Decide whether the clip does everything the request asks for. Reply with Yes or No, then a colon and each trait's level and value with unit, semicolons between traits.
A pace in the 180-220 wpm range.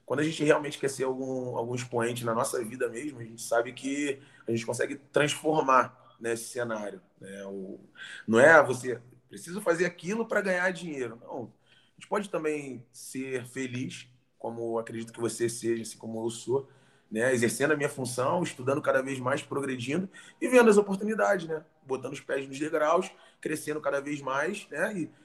Yes: fast, 185 wpm